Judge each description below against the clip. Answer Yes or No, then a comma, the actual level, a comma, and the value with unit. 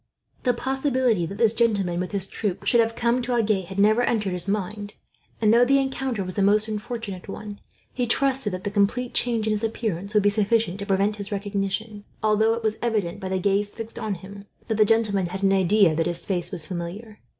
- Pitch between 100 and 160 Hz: No, high, 210 Hz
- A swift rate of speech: Yes, fast, 215 wpm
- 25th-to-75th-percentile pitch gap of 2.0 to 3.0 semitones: Yes, average, 2.7 semitones